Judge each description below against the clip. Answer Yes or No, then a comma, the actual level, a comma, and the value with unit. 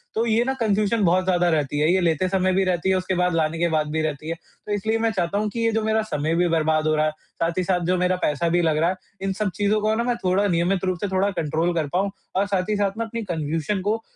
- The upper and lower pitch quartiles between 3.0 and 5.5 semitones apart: Yes, average, 3.8 semitones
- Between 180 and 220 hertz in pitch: Yes, medium, 185 Hz